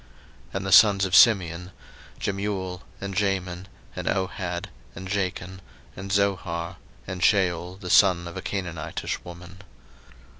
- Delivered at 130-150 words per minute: Yes, slow, 135 wpm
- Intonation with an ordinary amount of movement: No, narrow, 1.8 semitones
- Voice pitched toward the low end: Yes, very low, 95 Hz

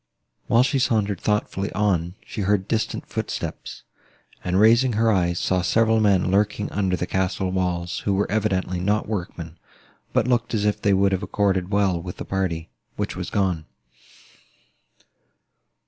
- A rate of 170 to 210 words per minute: No, average, 155 wpm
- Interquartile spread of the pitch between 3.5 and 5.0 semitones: No, narrow, 2.5 semitones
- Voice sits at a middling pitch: No, low, 100 Hz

